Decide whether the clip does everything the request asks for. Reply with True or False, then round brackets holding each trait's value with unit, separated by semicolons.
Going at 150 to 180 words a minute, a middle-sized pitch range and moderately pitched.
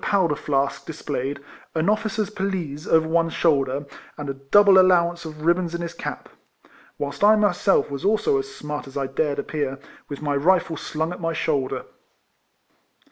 True (170 wpm; 4.2 semitones; 160 Hz)